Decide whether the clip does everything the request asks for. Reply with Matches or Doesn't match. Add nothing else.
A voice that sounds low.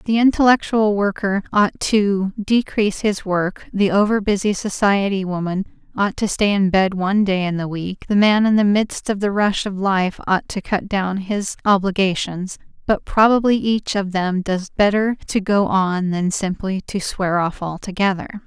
Doesn't match